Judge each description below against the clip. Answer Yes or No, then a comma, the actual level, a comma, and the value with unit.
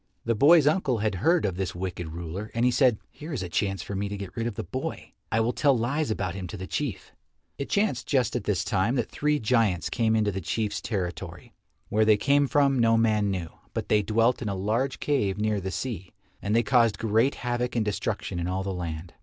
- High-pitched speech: No, low, 110 Hz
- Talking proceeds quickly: Yes, fast, 235 wpm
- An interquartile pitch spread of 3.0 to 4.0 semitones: No, average, 4.4 semitones